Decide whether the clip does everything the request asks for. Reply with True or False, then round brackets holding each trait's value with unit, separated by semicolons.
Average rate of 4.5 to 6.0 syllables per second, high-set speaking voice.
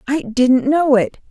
False (3.8 syllables/s; 255 Hz)